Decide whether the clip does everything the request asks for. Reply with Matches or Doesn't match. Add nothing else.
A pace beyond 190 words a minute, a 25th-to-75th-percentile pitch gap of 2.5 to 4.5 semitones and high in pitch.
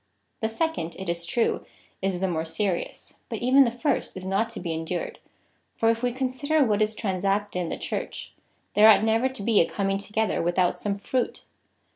Matches